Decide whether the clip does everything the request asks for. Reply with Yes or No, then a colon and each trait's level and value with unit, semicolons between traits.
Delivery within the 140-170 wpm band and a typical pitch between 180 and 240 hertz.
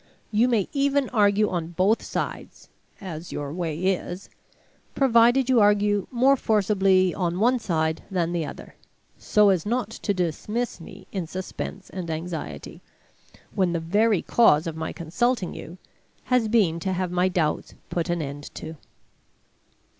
Yes: average, 150 wpm; high, 190 Hz